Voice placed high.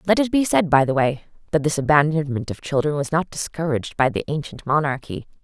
No: medium, 150 Hz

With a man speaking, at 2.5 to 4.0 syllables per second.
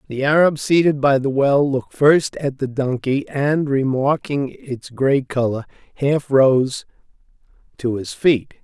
Yes: male; 3.9 syllables/s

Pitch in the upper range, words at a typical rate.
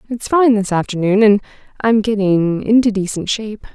Yes: high, 210 Hz; average, 160 wpm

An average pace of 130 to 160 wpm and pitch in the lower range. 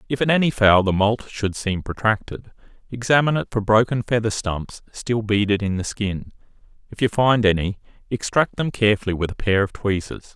No: average, 185 wpm; low, 110 Hz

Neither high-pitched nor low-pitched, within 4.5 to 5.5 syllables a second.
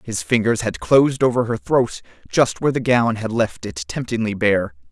No: low, 115 Hz; 5.0 syllables/s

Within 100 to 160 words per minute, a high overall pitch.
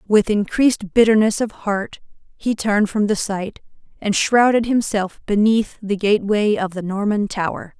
Yes: average, 155 wpm; high, 210 Hz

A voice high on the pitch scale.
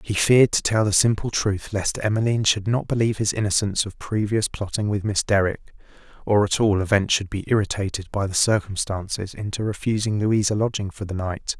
No: low, 105 Hz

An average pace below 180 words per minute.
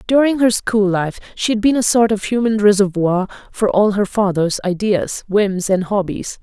No: average, 185 wpm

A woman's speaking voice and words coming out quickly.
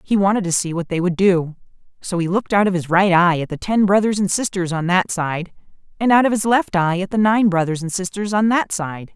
Yes: female; fast, 260 wpm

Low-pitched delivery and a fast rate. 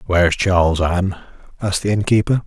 No: very low, 95 Hz; average, 170 wpm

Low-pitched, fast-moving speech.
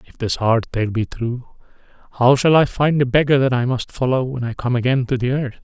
Yes: low, 125 Hz; fast, 245 wpm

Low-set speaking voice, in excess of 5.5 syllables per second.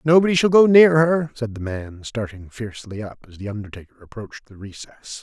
Yes: low, 120 Hz; 5.8 syllables/s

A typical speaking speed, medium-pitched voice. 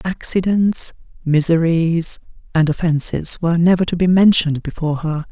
No: slow, 125 wpm; medium, 165 Hz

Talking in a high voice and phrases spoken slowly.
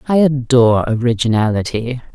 No: low, 125 Hz; slow, 85 wpm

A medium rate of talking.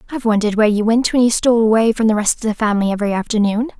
No: fast, 270 wpm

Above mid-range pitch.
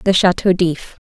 No: medium, 180 Hz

